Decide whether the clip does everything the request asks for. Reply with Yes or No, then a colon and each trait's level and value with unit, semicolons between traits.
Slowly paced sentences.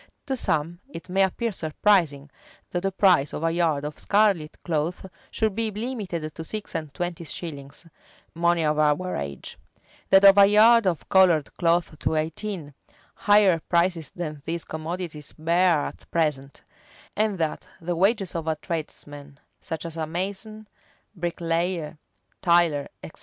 No: average, 150 wpm